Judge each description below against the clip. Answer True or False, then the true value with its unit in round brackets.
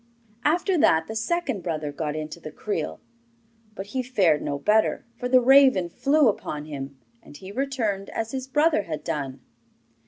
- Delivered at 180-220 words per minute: False (165 wpm)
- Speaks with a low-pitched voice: False (205 Hz)